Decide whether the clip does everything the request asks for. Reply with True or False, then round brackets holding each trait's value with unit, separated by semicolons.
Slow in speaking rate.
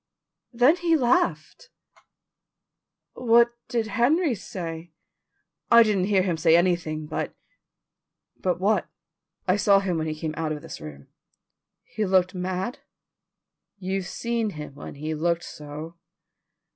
True (130 wpm)